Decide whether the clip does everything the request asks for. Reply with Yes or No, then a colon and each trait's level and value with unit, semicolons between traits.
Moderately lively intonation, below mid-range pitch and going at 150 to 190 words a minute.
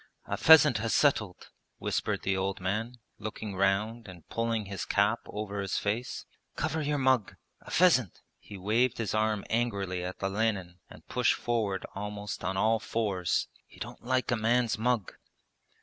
Yes: average, 3.3 semitones; low, 110 Hz; average, 160 wpm